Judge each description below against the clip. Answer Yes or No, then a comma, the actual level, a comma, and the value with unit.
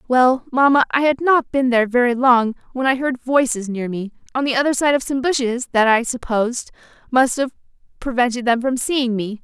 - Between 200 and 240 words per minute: Yes, fast, 205 wpm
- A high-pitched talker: Yes, very high, 250 Hz